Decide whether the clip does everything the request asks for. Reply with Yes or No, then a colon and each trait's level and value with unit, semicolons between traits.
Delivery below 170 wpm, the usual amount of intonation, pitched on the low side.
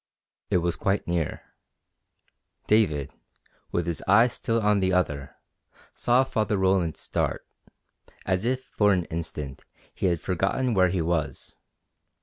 Yes: slow, 135 wpm; average, 4.0 semitones; very low, 95 Hz